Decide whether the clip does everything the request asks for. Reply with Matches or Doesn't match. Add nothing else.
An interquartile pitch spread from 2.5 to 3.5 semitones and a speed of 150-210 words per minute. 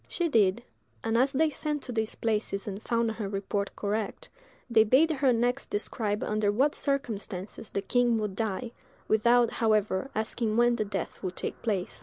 Matches